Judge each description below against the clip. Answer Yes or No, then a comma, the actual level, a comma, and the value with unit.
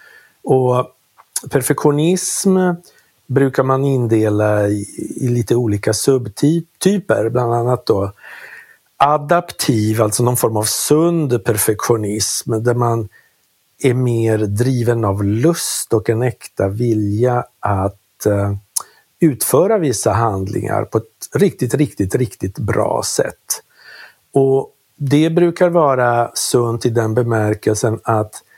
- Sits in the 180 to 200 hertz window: No, low, 120 Hz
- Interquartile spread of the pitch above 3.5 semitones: Yes, average, 4.2 semitones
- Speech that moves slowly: Yes, slow, 105 wpm